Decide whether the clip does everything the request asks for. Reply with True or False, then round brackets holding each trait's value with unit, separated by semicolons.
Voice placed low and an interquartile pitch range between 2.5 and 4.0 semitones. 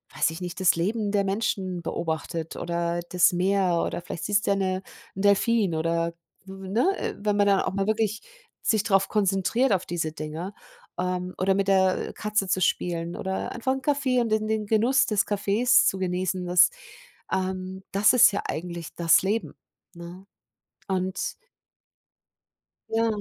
False (190 Hz; 2.9 semitones)